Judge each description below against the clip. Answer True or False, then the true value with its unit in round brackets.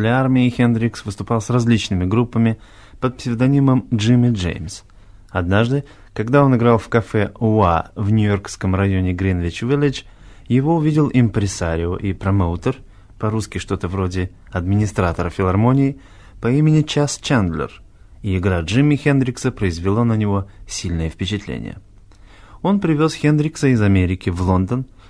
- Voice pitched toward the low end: True (105 Hz)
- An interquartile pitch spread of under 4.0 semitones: False (4.7 semitones)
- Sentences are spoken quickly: False (125 wpm)